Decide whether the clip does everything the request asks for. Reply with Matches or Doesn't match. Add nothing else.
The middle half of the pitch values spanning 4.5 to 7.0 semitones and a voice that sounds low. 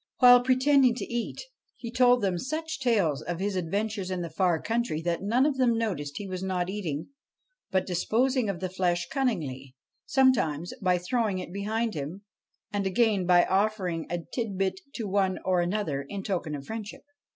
Doesn't match